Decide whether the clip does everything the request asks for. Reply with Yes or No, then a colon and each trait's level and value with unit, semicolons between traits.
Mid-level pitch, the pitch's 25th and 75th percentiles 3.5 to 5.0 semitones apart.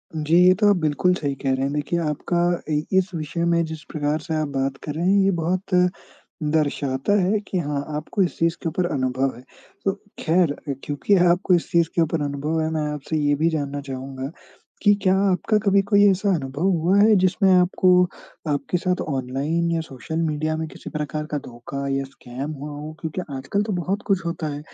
Yes: medium, 155 Hz; average, 4.0 semitones